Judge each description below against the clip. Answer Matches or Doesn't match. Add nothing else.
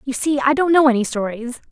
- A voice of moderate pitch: Doesn't match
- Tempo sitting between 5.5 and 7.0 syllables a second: Matches